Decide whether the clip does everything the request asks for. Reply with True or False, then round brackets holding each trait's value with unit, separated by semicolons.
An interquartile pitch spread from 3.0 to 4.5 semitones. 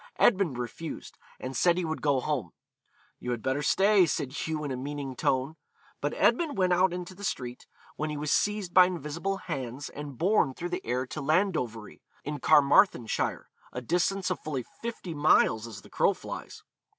False (5.5 semitones)